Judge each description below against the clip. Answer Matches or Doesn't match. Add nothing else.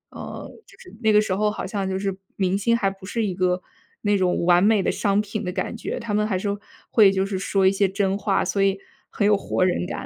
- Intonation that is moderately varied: Doesn't match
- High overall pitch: Matches